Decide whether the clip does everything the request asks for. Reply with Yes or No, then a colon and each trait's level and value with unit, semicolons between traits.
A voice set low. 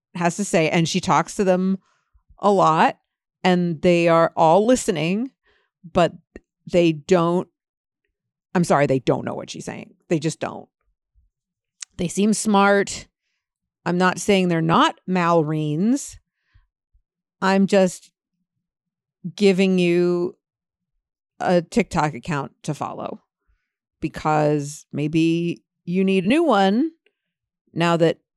No: medium, 180 Hz